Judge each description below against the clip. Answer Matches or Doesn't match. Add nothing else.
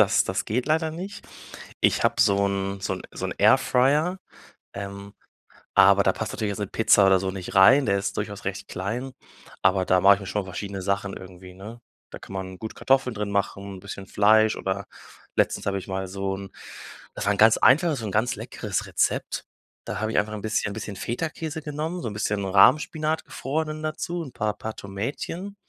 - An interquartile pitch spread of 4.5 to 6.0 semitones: Matches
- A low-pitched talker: Matches